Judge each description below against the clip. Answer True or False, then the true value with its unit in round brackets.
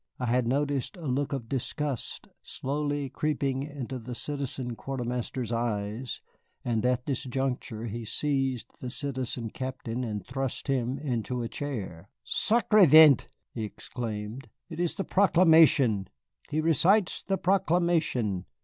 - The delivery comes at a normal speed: False (130 wpm)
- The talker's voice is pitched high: False (130 Hz)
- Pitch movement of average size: True (3.8 semitones)